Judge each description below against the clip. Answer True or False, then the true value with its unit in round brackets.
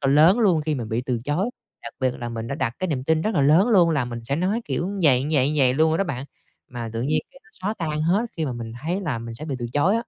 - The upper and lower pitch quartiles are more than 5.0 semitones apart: True (5.6 semitones)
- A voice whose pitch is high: False (150 Hz)